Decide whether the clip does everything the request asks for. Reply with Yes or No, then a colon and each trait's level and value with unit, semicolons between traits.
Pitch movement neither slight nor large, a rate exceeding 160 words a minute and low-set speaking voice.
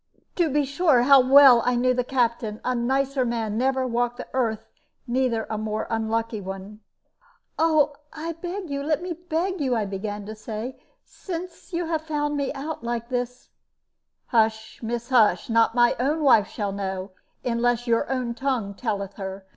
No: average, 4.2 semitones; average, 170 wpm; high, 245 Hz